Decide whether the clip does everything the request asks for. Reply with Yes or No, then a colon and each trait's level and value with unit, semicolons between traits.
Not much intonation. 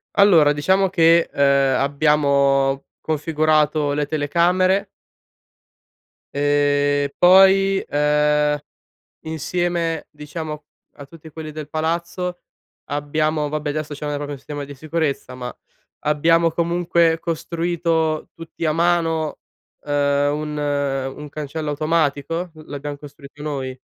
Yes: narrow, 2.3 semitones